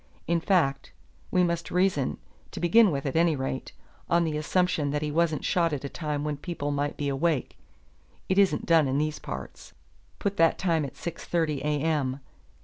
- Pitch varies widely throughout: No, average, 2.9 semitones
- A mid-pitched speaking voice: Yes, medium, 155 Hz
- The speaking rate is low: No, average, 190 wpm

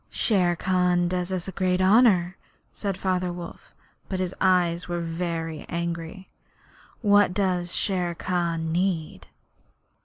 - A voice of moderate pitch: Yes, medium, 180 Hz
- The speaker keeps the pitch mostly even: Yes, narrow, 1.6 semitones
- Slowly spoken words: Yes, slow, 120 wpm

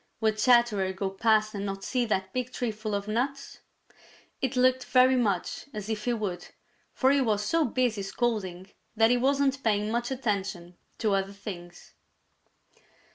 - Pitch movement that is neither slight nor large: Yes, average, 4.0 semitones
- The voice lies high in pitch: Yes, high, 220 Hz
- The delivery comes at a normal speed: Yes, average, 165 wpm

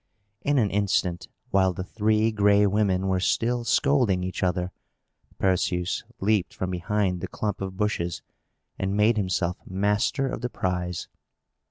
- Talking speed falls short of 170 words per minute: Yes, average, 145 wpm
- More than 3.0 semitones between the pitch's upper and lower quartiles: No, average, 2.7 semitones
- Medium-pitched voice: No, very low, 95 Hz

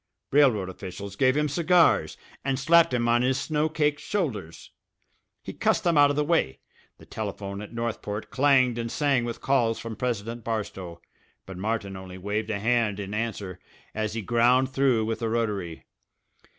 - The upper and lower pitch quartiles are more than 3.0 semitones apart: Yes, average, 4.8 semitones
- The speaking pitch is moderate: No, low, 115 Hz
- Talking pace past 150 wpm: Yes, average, 170 wpm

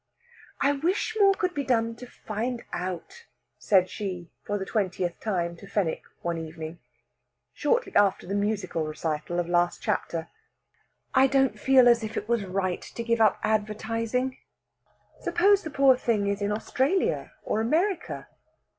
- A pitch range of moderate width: No, wide, 6.2 semitones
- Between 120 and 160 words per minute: Yes, average, 155 wpm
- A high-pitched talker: Yes, high, 215 Hz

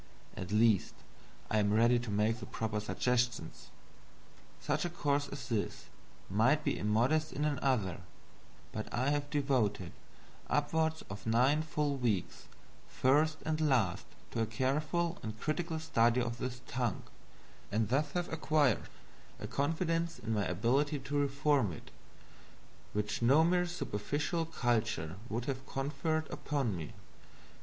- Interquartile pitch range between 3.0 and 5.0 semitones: No, wide, 5.4 semitones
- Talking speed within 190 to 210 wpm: No, slow, 135 wpm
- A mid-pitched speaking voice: No, low, 130 Hz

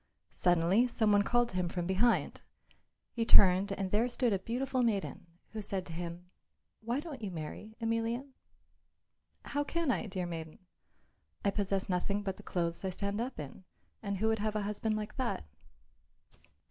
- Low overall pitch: No, high, 205 Hz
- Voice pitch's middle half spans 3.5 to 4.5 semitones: Yes, average, 3.9 semitones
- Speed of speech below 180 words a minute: Yes, average, 170 wpm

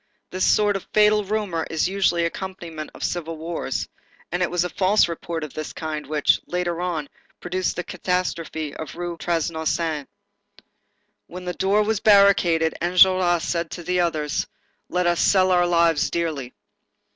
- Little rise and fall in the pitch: Yes, narrow, 2.3 semitones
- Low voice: No, medium, 175 Hz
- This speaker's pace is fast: No, average, 165 wpm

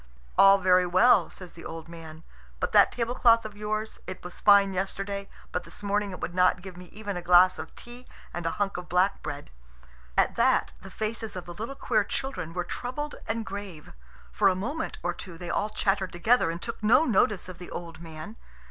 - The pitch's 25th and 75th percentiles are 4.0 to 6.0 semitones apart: No, average, 3.5 semitones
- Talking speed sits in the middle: No, fast, 210 wpm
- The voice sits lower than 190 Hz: No, high, 195 Hz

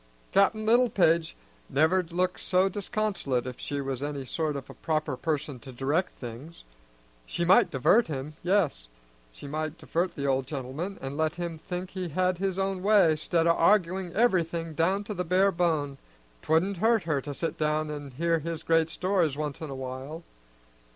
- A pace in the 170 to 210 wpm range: Yes, average, 180 wpm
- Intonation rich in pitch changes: No, average, 4.3 semitones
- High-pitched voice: No, medium, 165 Hz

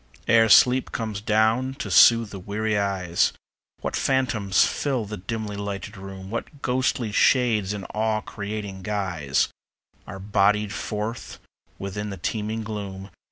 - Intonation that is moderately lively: No, narrow, 2.3 semitones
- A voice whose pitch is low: Yes, low, 105 Hz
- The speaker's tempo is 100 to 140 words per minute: Yes, slow, 135 wpm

